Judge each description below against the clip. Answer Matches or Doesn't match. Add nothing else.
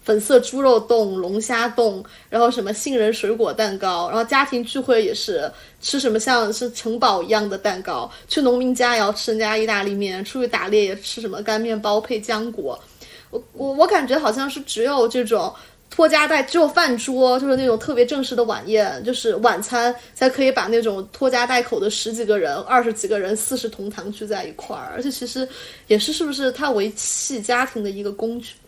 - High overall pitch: Matches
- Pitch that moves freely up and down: Doesn't match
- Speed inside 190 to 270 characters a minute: Doesn't match